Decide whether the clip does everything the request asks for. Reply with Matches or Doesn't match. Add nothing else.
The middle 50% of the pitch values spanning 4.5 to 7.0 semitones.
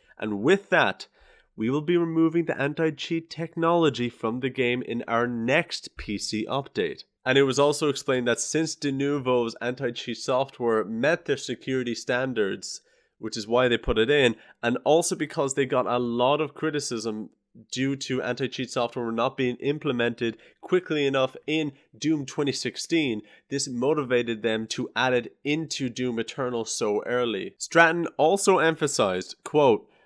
Doesn't match